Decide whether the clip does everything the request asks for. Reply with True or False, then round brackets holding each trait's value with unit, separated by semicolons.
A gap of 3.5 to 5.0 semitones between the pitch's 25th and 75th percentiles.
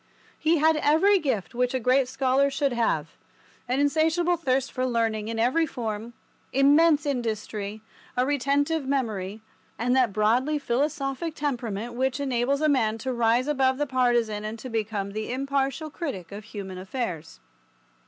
True (4.1 semitones)